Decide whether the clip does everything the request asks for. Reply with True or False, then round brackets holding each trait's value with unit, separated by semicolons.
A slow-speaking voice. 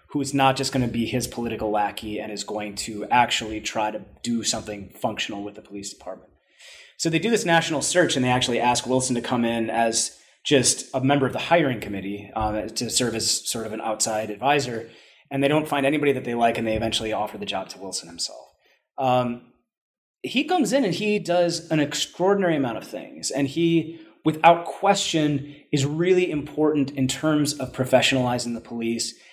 False (195 wpm)